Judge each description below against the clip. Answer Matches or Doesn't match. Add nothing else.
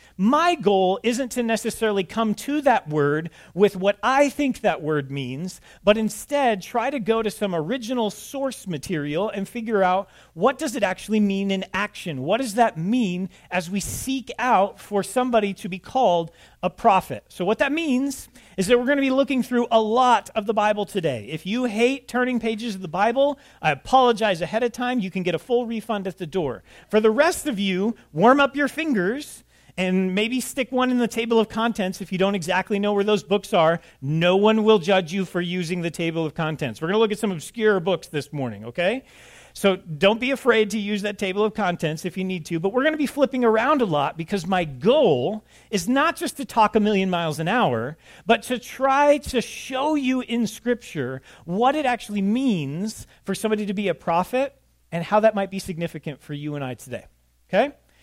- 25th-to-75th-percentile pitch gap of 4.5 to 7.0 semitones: Matches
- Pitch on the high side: Matches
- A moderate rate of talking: Doesn't match